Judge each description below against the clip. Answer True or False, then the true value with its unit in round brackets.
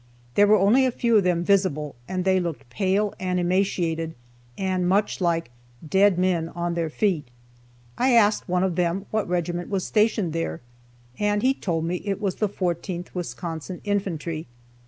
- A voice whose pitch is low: False (180 Hz)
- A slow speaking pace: False (170 wpm)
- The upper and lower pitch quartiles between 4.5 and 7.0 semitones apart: False (3.0 semitones)